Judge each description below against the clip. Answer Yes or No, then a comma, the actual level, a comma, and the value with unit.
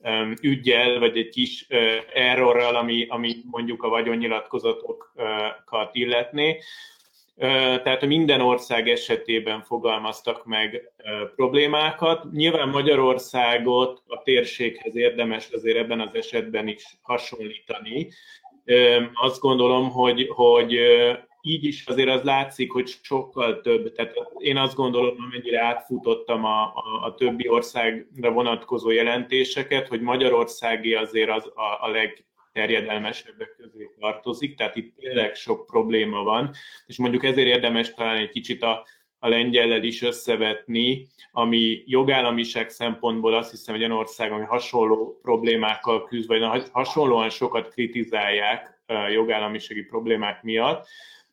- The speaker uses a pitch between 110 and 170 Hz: Yes, low, 120 Hz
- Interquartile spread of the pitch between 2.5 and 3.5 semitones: Yes, average, 2.8 semitones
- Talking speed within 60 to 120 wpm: Yes, average, 115 wpm